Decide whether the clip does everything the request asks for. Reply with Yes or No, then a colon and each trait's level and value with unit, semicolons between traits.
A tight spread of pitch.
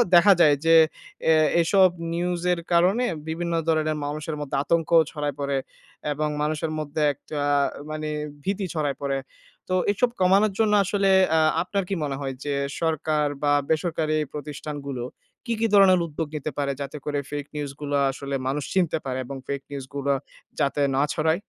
No: average, 3.1 semitones